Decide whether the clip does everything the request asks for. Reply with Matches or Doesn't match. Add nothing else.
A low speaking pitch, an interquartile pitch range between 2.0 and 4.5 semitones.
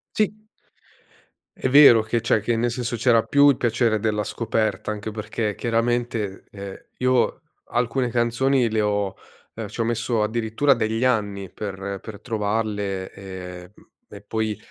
Matches